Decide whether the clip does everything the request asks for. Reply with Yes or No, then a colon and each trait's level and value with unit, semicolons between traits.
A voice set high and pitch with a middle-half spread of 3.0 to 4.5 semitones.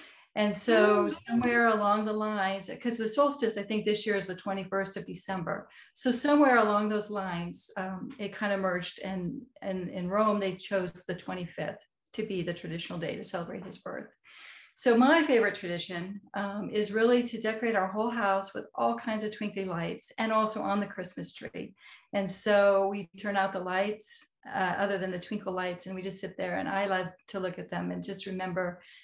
No: high, 200 Hz; narrow, 2.5 semitones